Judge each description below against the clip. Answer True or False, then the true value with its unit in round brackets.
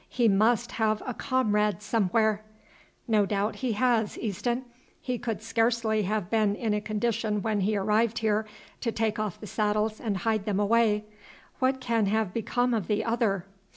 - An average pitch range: False (1.8 semitones)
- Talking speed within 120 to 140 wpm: False (170 wpm)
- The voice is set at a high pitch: True (220 Hz)